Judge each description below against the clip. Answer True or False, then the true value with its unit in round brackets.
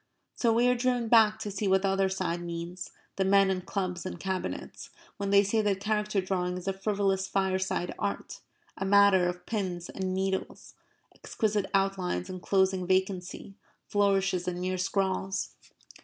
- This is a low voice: False (190 Hz)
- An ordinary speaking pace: True (160 wpm)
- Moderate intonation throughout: False (1.6 semitones)